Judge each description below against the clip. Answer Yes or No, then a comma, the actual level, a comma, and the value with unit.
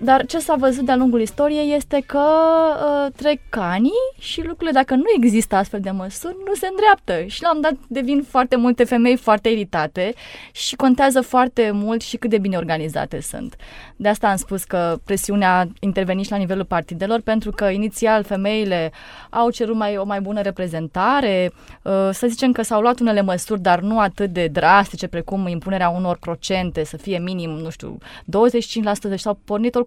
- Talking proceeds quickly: Yes, fast, 185 wpm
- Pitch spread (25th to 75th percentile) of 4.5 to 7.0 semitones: Yes, average, 5.1 semitones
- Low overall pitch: No, high, 215 Hz